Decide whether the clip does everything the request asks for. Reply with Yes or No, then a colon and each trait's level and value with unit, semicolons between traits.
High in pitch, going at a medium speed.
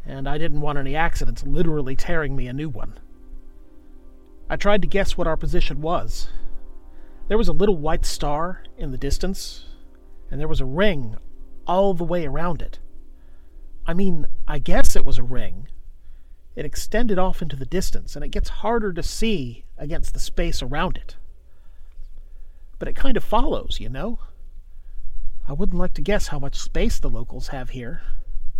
No: medium, 140 Hz; average, 175 wpm